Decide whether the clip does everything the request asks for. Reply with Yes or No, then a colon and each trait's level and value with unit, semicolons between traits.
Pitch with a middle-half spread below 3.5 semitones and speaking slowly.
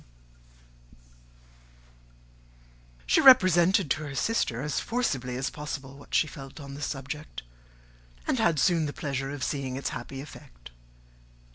Yes: narrow, 2.6 semitones; slow, 130 wpm